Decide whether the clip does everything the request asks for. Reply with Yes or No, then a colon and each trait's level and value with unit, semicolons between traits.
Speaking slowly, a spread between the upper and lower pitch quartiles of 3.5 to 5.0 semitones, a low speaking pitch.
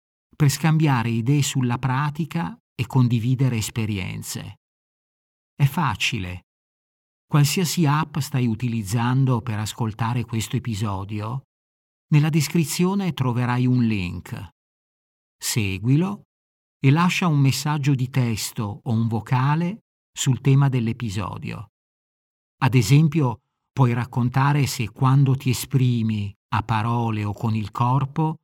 Yes: slow, 105 wpm; average, 4.4 semitones; low, 125 Hz